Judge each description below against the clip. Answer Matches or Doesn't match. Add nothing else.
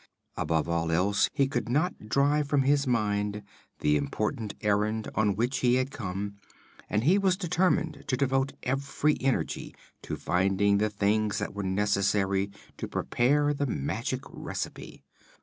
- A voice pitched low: Matches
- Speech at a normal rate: Matches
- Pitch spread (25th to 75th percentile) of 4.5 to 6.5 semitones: Matches